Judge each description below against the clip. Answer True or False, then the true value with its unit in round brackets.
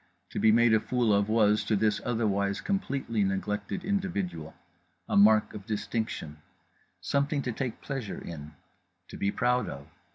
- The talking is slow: False (155 wpm)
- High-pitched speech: False (110 Hz)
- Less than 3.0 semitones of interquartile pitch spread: False (3.7 semitones)